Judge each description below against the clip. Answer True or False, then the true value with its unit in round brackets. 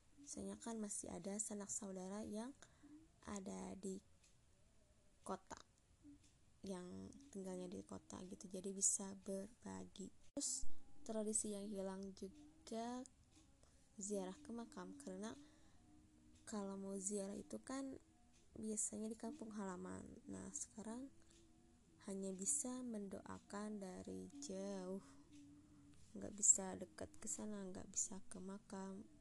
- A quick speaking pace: False (105 wpm)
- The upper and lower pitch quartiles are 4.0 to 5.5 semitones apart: False (3.0 semitones)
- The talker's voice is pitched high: True (195 Hz)